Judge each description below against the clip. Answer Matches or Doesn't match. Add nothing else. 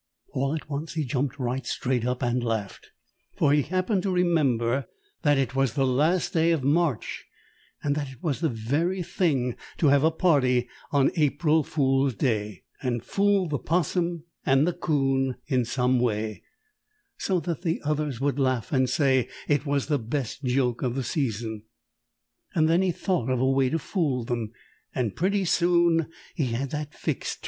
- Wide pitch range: Doesn't match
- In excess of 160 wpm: Matches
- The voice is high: Doesn't match